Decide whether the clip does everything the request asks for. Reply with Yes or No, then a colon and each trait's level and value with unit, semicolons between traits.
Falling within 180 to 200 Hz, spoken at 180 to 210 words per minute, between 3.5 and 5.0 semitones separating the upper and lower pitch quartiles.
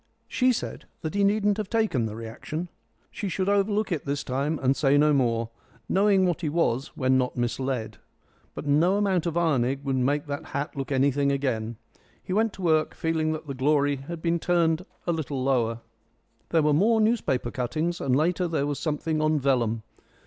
No: medium, 150 Hz; average, 190 wpm; average, 4.6 semitones